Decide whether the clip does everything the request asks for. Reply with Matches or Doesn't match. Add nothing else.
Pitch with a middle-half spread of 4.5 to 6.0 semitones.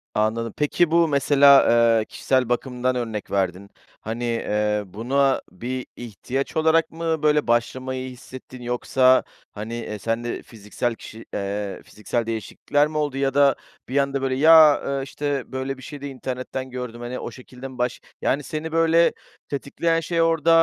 Doesn't match